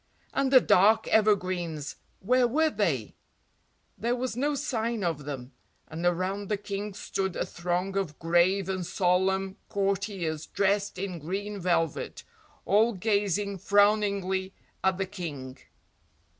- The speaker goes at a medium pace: No, slow, 130 wpm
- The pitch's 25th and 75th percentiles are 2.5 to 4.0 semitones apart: Yes, average, 2.9 semitones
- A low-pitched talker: No, high, 195 Hz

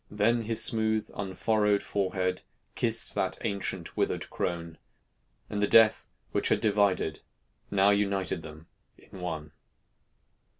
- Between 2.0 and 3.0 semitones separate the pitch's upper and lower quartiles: Yes, average, 2.7 semitones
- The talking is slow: Yes, slow, 120 wpm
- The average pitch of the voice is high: No, low, 100 Hz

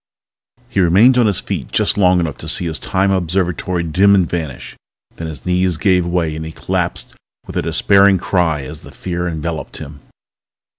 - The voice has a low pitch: Yes, very low, 90 Hz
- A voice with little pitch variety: No, average, 3.0 semitones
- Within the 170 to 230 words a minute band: Yes, average, 185 wpm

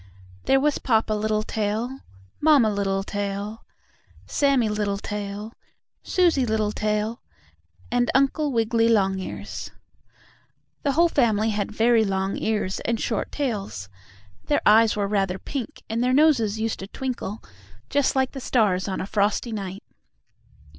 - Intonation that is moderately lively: Yes, average, 3.7 semitones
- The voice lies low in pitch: No, high, 220 Hz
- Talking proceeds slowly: Yes, slow, 125 wpm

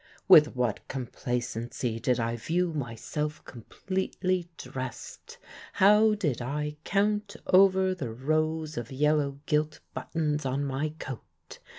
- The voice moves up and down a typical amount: No, wide, 5.8 semitones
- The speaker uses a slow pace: Yes, slow, 115 wpm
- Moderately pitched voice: Yes, medium, 150 Hz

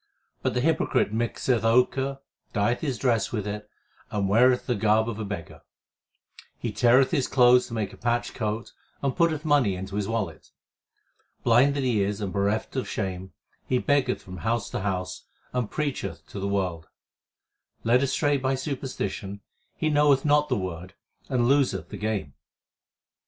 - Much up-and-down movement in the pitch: No, average, 4.8 semitones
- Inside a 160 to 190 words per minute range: Yes, average, 165 wpm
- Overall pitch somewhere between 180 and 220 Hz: No, low, 115 Hz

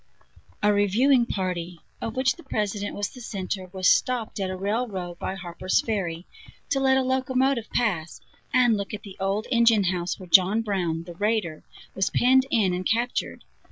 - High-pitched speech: Yes, high, 205 Hz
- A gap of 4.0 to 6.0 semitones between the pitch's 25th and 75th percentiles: Yes, average, 4.5 semitones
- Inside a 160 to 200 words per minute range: Yes, average, 175 wpm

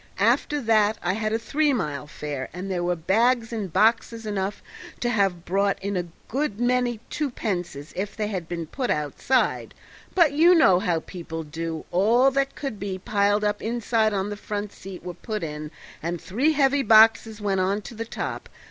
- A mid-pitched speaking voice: No, high, 205 Hz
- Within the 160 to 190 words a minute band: Yes, average, 185 wpm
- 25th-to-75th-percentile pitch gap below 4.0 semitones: No, average, 4.6 semitones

